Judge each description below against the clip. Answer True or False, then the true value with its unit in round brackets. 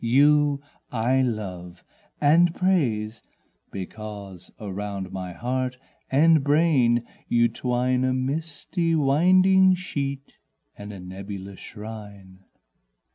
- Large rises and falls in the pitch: True (6.3 semitones)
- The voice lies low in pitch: True (125 Hz)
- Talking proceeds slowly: True (95 wpm)